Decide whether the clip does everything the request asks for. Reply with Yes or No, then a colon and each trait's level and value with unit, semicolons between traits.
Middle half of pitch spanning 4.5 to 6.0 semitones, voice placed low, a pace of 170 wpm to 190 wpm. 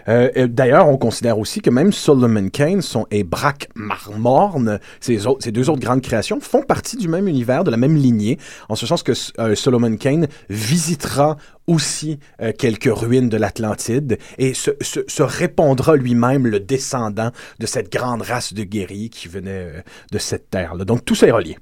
Yes: average, 4.9 semitones; low, 125 Hz; average, 185 wpm